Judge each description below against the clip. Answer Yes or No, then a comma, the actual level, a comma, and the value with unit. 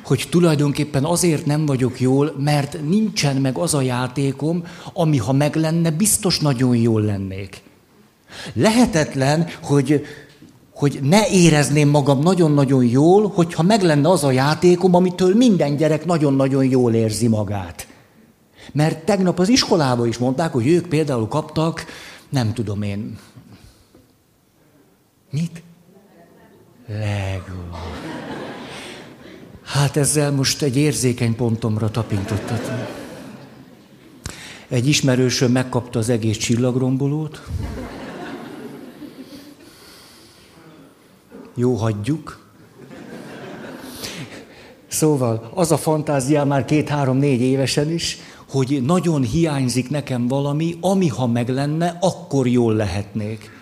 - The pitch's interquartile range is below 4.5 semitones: No, average, 4.9 semitones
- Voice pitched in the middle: Yes, medium, 145 Hz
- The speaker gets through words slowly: Yes, slow, 100 wpm